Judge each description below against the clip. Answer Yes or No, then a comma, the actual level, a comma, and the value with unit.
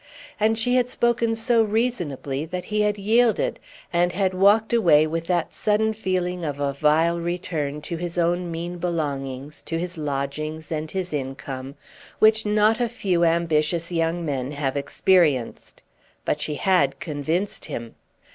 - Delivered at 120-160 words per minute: Yes, average, 155 wpm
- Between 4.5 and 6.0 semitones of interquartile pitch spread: Yes, wide, 5.4 semitones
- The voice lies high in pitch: No, medium, 170 Hz